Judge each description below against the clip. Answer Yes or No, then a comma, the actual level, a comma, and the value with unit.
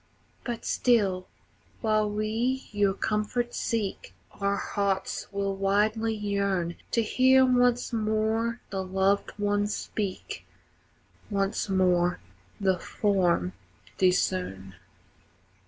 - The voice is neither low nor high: No, high, 205 Hz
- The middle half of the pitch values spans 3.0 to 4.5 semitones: No, narrow, 2.5 semitones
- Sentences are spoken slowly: Yes, slow, 95 wpm